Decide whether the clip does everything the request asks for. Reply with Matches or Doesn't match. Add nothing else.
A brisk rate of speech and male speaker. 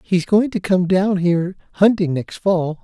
Doesn't match